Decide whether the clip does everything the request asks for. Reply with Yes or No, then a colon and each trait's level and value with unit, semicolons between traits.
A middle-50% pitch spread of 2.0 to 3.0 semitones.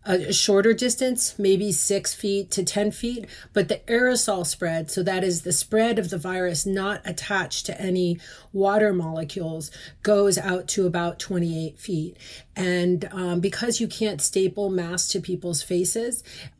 Yes: narrow, 2.5 semitones